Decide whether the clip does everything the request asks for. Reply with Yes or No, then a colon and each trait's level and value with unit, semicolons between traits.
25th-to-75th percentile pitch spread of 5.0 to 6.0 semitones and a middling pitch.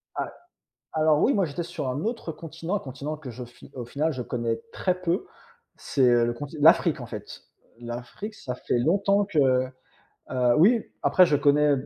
Yes: wide, 5.4 semitones; medium, 150 Hz